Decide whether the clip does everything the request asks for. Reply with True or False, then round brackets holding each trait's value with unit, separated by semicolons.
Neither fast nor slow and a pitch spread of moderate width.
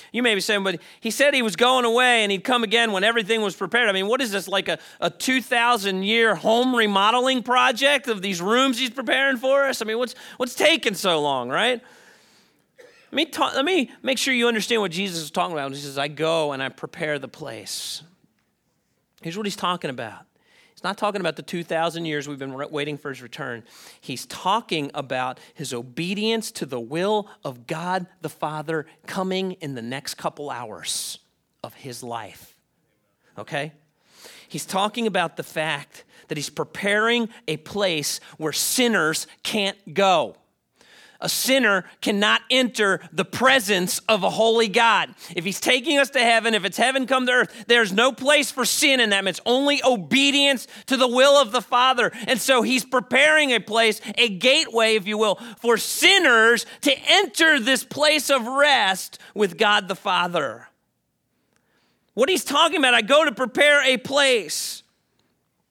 False (180 wpm; 6.9 semitones)